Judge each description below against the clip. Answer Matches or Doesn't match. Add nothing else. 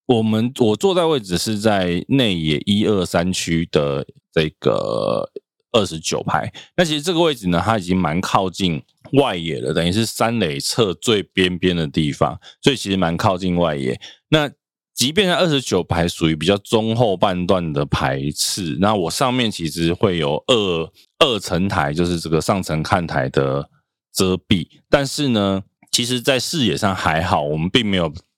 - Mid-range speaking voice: Doesn't match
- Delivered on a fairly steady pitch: Doesn't match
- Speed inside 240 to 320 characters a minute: Matches